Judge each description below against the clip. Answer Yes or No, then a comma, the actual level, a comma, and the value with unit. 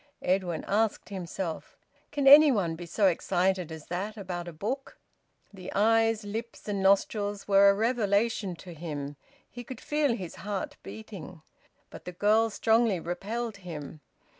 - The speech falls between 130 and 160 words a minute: Yes, average, 150 wpm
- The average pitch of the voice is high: Yes, high, 200 Hz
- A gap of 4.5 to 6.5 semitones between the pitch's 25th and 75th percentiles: No, average, 4.1 semitones